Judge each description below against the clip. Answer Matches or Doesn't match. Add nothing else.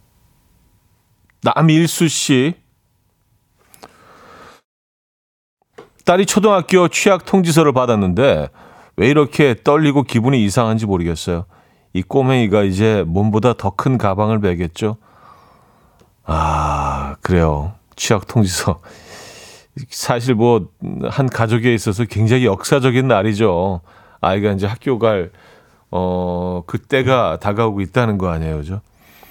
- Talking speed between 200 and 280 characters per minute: Matches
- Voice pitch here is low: Matches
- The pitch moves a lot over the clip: Matches